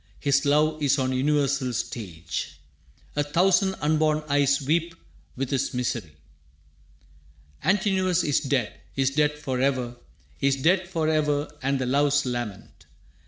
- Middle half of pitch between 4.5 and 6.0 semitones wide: No, average, 2.9 semitones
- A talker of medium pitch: Yes, medium, 145 Hz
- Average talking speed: No, slow, 125 wpm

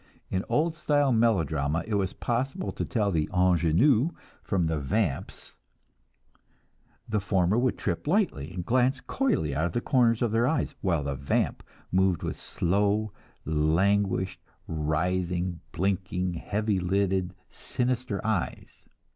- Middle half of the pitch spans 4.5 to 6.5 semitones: Yes, average, 5.2 semitones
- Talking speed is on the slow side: Yes, slow, 130 wpm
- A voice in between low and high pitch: No, very low, 95 Hz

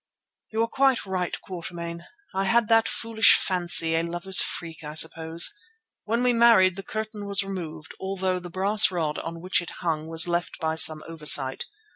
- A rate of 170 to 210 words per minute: Yes, average, 175 wpm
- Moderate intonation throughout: Yes, average, 3.7 semitones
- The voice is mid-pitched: Yes, medium, 180 Hz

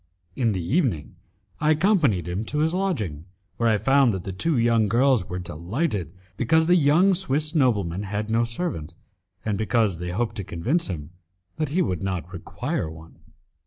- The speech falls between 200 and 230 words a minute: No, average, 175 wpm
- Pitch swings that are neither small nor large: No, wide, 8.8 semitones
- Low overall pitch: Yes, low, 115 Hz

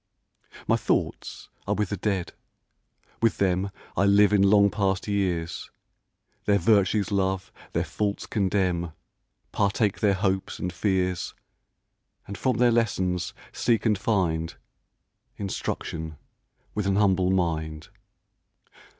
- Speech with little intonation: Yes, narrow, 2.3 semitones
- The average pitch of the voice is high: No, very low, 95 Hz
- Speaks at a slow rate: Yes, slow, 115 wpm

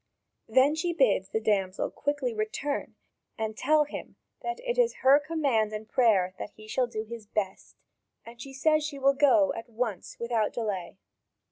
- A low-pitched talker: No, high, 240 Hz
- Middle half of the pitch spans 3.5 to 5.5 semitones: Yes, average, 5.2 semitones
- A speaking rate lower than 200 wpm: Yes, average, 175 wpm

